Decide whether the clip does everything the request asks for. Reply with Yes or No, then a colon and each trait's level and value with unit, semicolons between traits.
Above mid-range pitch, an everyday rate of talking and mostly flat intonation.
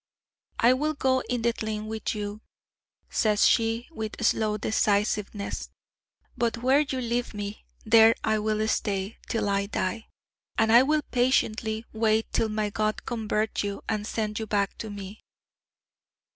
Yes: high, 220 Hz; average, 150 wpm; narrow, 1.7 semitones